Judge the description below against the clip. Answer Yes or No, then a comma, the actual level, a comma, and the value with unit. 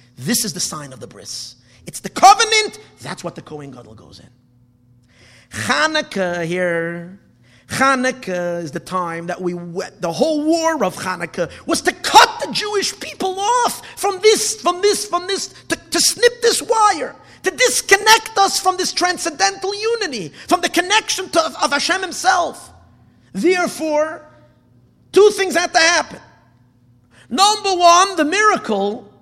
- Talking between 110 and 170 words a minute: Yes, average, 150 wpm